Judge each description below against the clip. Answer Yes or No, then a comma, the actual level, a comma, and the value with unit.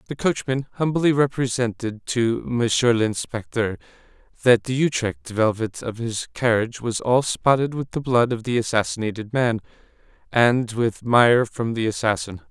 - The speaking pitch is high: No, low, 120 Hz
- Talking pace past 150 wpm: No, average, 145 wpm